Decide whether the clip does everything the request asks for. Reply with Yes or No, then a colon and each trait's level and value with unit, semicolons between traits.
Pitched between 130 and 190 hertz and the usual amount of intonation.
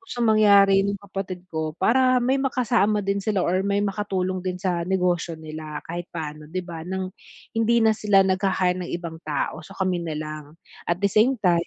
Yes: medium, 185 Hz; average, 3.2 semitones